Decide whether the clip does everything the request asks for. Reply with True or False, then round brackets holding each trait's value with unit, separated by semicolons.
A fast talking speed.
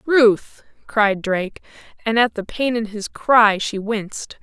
False (165 wpm)